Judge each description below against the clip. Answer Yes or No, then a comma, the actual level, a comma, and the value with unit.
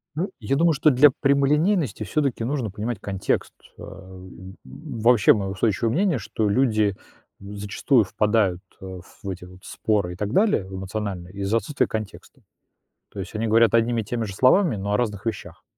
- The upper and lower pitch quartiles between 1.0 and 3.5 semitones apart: No, average, 4.8 semitones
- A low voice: Yes, low, 110 Hz